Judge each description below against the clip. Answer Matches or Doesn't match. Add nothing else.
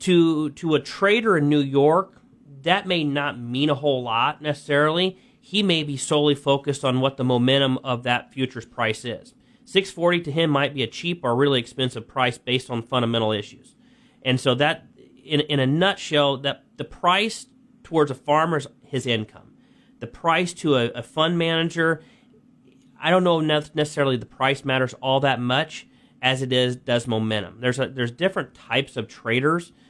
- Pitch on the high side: Doesn't match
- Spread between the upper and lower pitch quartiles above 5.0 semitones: Doesn't match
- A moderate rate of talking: Matches